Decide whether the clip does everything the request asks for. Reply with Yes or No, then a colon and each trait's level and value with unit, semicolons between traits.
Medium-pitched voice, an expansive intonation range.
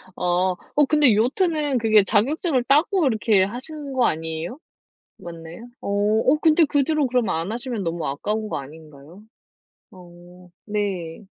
No: high, 215 Hz; wide, 7.7 semitones